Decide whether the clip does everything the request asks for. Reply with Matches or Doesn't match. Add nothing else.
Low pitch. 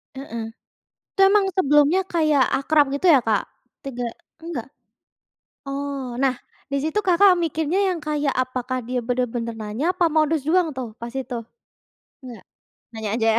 Doesn't match